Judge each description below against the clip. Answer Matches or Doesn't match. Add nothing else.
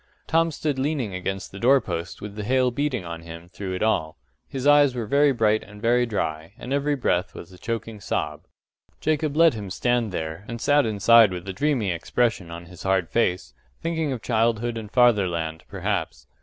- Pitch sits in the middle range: Doesn't match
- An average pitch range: Doesn't match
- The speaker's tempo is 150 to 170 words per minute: Doesn't match